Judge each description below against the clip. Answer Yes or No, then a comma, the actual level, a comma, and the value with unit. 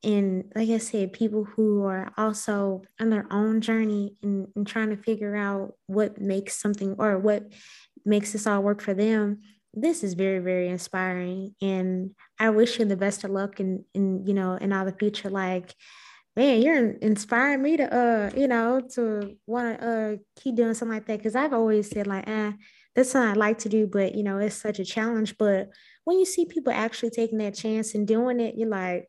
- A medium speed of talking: No, fast, 210 wpm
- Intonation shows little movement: Yes, narrow, 2.3 semitones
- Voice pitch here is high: Yes, high, 210 Hz